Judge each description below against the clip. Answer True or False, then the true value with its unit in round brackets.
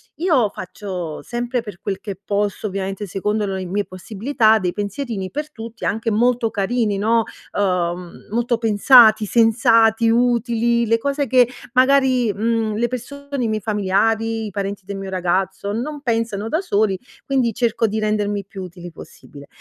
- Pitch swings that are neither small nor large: True (3.1 semitones)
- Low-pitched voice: False (220 Hz)